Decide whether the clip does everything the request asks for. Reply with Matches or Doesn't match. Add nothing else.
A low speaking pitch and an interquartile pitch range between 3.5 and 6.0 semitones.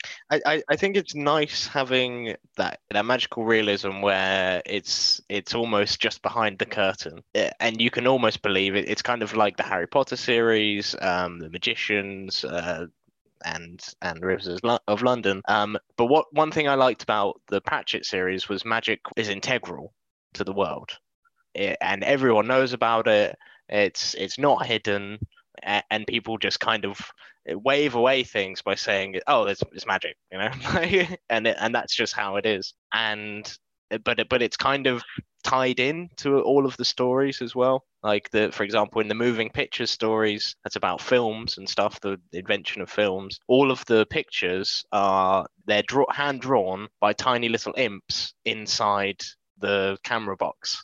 Matches